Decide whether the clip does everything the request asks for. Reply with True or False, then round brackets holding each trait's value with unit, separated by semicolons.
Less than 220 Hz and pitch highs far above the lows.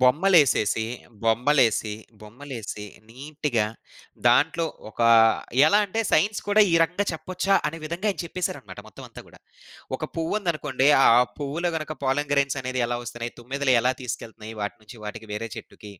True (135 Hz; 5.9 semitones)